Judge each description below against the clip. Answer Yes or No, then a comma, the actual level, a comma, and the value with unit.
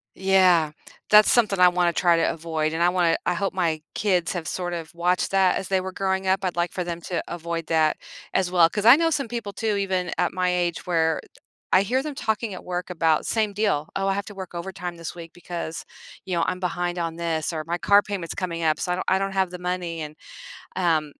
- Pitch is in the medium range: Yes, medium, 180 Hz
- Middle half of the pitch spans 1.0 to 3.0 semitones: Yes, narrow, 2.4 semitones